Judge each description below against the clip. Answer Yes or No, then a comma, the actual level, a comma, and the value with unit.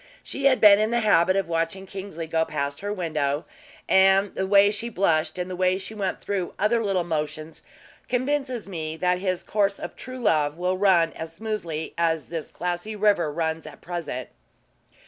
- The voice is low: No, medium, 185 Hz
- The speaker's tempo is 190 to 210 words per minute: No, average, 175 wpm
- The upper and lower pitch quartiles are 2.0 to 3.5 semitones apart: No, average, 4.0 semitones